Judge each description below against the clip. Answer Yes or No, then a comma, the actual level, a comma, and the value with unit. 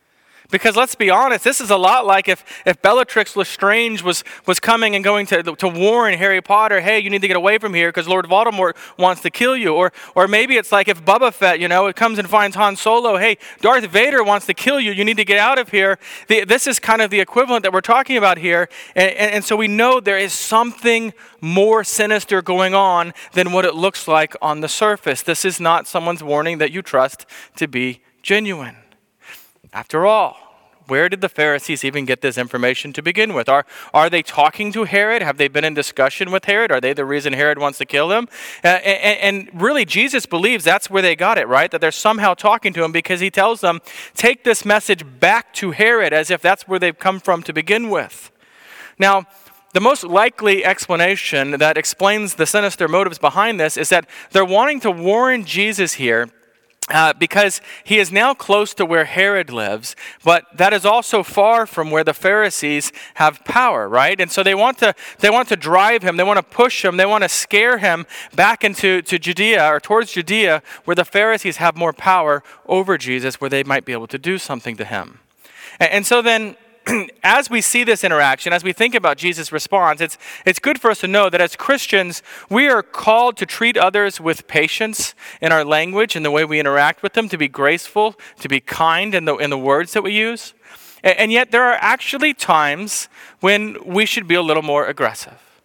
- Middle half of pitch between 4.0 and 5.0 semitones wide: Yes, average, 4.7 semitones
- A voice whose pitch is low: No, high, 190 Hz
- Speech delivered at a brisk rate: Yes, fast, 215 wpm